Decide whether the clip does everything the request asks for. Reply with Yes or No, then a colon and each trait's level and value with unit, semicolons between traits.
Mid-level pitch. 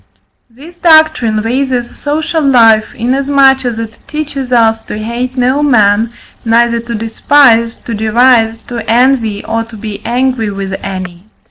No: high, 235 Hz